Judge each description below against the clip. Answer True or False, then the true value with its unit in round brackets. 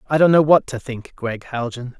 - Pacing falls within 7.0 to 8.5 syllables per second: False (5.0 syllables/s)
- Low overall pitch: True (130 Hz)